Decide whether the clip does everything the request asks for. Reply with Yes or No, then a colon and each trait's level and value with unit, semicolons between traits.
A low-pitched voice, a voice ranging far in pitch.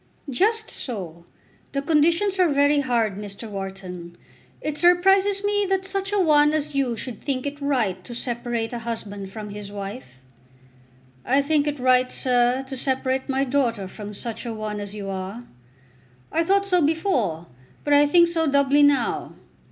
No: very high, 260 Hz; wide, 6.3 semitones